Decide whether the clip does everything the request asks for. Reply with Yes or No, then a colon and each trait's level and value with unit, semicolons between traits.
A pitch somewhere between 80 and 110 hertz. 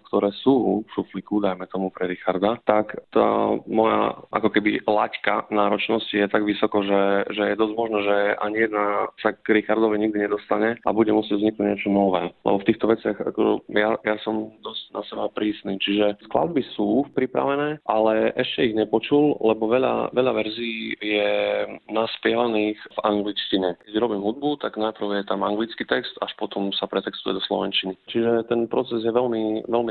Yes: low, 105 Hz